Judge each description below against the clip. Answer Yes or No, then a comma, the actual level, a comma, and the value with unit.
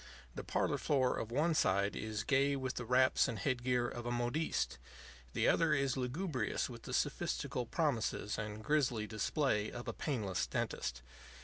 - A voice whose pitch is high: No, low, 125 Hz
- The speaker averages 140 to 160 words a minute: No, average, 170 wpm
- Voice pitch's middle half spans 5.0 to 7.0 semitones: No, average, 4.2 semitones